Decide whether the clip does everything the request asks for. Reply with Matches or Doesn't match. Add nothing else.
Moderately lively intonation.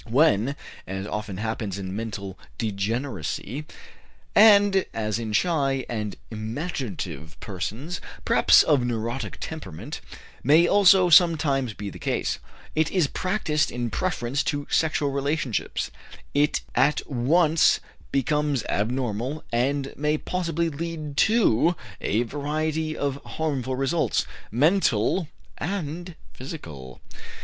Doesn't match